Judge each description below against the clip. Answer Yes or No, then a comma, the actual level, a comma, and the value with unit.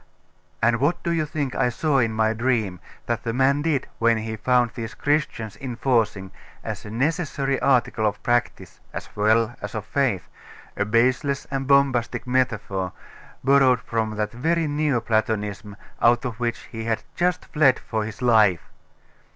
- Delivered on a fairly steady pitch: No, average, 3.8 semitones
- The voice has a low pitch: Yes, low, 120 Hz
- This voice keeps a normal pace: Yes, average, 160 wpm